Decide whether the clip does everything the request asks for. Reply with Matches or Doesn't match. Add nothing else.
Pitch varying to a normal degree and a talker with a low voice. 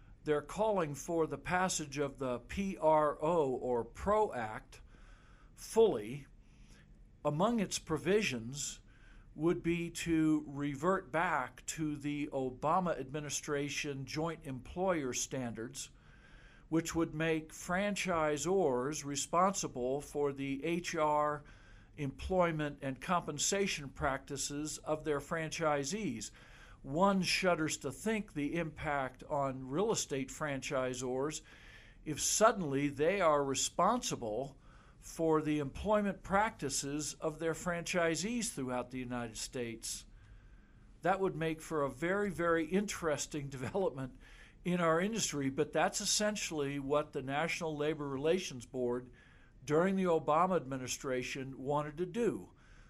Doesn't match